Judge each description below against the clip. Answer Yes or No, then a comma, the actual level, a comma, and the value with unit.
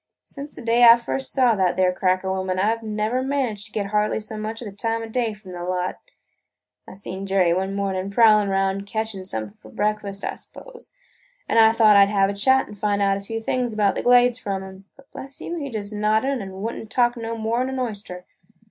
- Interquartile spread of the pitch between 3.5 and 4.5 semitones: No, average, 3.0 semitones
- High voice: Yes, high, 210 Hz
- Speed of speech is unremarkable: No, fast, 235 wpm